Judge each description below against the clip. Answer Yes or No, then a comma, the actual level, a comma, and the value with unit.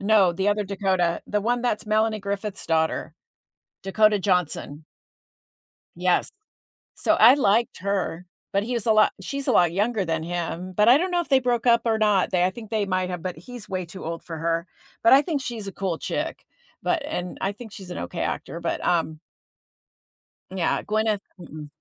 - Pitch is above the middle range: Yes, high, 195 Hz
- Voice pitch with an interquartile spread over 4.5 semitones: No, average, 3.8 semitones